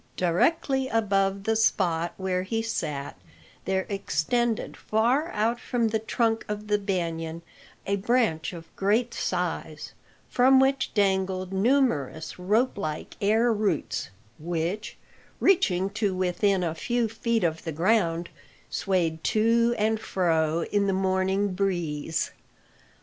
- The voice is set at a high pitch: Yes, high, 195 Hz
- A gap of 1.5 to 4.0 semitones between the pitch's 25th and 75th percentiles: No, average, 4.5 semitones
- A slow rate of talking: Yes, slow, 125 wpm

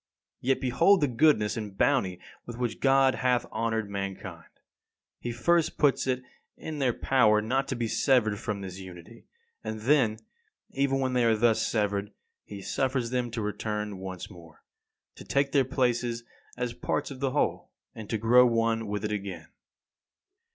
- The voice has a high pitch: No, low, 115 Hz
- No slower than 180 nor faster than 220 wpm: No, average, 165 wpm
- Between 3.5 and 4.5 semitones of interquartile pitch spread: Yes, average, 3.8 semitones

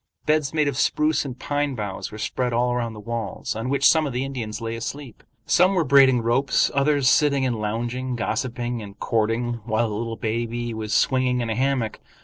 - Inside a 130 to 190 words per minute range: No, average, 200 wpm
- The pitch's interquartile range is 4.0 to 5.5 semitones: No, average, 3.2 semitones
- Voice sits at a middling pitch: No, low, 120 Hz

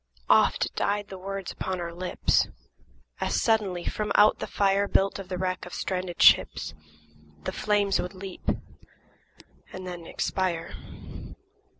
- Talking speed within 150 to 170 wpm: No, slow, 135 wpm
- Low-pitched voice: No, high, 190 Hz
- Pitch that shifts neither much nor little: No, narrow, 1.7 semitones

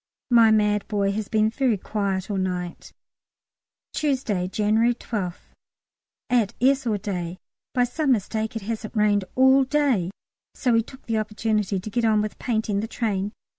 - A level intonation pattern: No, average, 3.0 semitones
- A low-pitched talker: No, high, 215 Hz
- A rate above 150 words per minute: Yes, average, 160 wpm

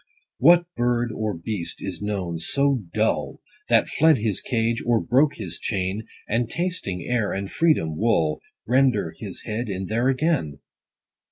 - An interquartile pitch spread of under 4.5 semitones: No, average, 5.0 semitones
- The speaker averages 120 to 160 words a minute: Yes, average, 155 wpm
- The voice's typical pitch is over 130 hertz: No, low, 115 Hz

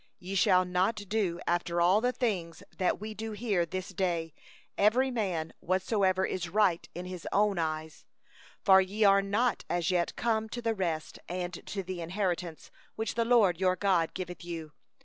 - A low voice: No, medium, 185 Hz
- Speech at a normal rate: Yes, average, 170 wpm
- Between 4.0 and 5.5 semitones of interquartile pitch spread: No, average, 3.3 semitones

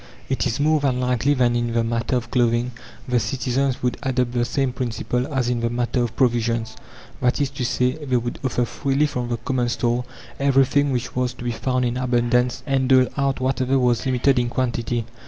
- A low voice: Yes, low, 125 Hz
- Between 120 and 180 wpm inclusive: No, fast, 205 wpm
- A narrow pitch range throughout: Yes, narrow, 1.7 semitones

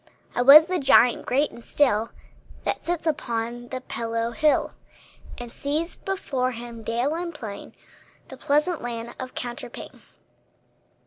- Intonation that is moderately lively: Yes, average, 4.3 semitones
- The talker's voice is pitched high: Yes, very high, 250 Hz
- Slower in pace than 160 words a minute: Yes, slow, 135 wpm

